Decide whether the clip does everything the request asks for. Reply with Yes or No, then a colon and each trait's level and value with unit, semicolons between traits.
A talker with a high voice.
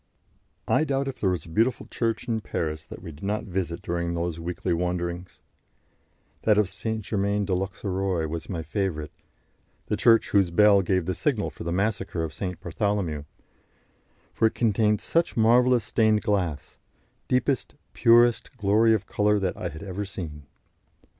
No: very low, 95 Hz